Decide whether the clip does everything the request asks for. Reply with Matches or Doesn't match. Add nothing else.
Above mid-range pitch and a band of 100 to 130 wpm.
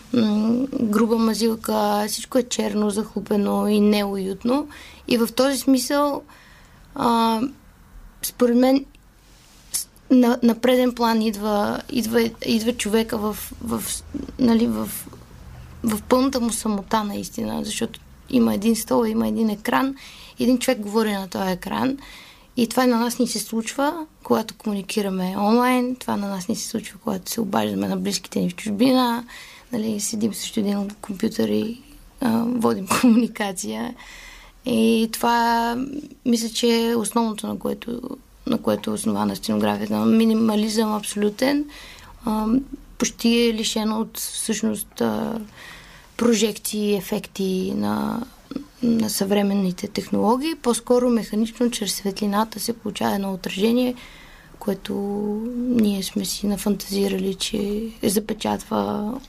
Matches